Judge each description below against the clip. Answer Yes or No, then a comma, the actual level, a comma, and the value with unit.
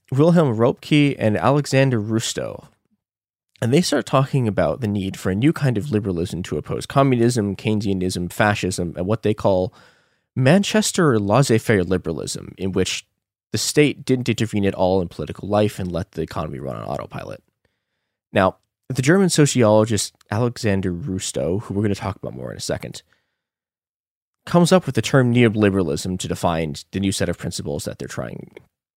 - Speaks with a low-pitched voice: Yes, low, 105 Hz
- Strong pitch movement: Yes, wide, 5.7 semitones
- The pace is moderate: Yes, average, 165 wpm